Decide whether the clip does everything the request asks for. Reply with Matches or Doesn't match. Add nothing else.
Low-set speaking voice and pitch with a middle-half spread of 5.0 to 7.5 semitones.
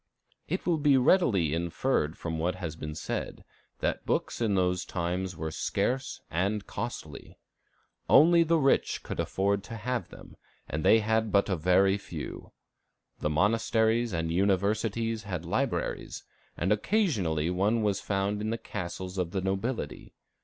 Doesn't match